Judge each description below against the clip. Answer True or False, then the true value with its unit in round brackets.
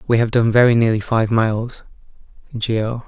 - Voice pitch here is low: True (115 Hz)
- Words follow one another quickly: False (155 wpm)